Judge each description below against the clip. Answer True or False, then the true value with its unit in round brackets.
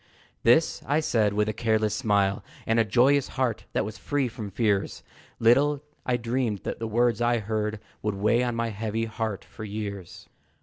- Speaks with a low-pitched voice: True (110 Hz)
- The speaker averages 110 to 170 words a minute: False (180 wpm)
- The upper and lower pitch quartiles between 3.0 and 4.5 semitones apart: False (2.4 semitones)